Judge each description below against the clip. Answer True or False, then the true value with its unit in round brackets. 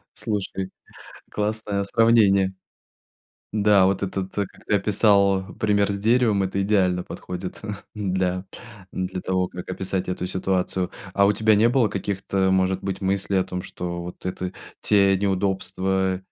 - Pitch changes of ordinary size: False (1.6 semitones)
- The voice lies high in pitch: False (95 Hz)